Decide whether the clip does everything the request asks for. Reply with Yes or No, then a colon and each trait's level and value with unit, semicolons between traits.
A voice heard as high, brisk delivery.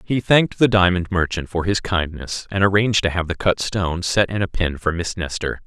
No: very low, 95 Hz; fast, 235 wpm